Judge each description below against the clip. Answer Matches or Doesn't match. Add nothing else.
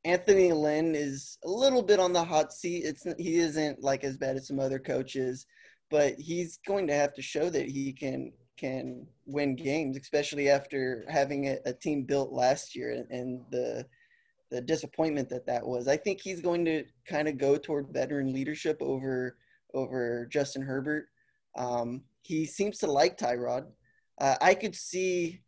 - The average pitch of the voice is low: Doesn't match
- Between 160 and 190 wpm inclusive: Matches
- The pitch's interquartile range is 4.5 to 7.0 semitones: Doesn't match